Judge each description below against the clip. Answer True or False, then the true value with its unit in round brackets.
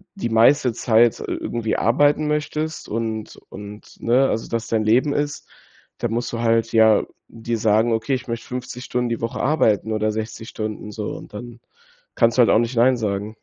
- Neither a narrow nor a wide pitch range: False (2.0 semitones)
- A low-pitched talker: True (115 Hz)